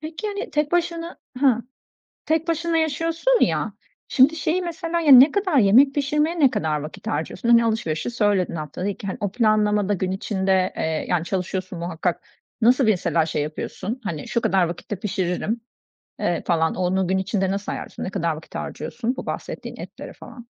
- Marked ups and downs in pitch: Yes, wide, 8.5 semitones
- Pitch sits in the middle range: No, high, 215 Hz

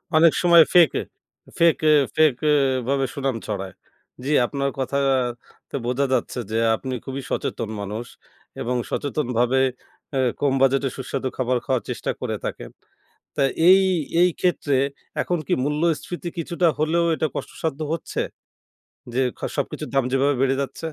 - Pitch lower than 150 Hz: Yes, low, 135 Hz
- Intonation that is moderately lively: Yes, average, 3.5 semitones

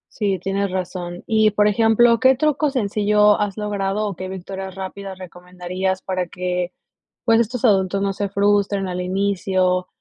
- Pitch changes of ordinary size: No, narrow, 2.1 semitones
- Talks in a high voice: Yes, high, 195 Hz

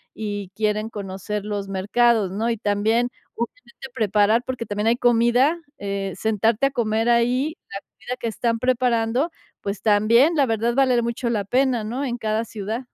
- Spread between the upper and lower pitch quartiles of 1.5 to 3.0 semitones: Yes, narrow, 2.6 semitones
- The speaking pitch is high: Yes, high, 225 Hz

